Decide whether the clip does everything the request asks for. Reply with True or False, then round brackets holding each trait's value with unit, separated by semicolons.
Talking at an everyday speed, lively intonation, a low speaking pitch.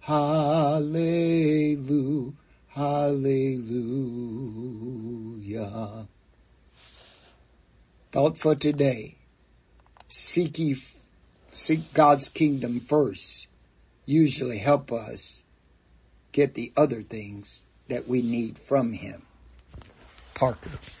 False (70 wpm; 5.8 semitones; 125 Hz)